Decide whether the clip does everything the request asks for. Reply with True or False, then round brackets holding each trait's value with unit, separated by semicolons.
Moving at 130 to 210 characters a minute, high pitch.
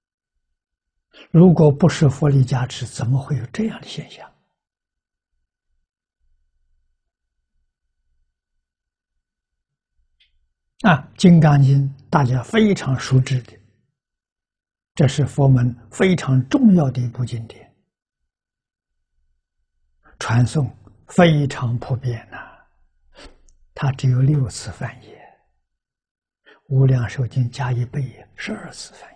False (140 characters per minute; 120 Hz)